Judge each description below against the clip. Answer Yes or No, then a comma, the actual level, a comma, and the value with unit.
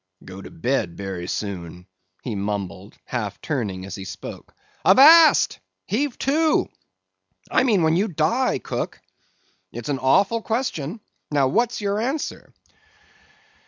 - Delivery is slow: Yes, slow, 125 wpm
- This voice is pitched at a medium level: Yes, medium, 145 Hz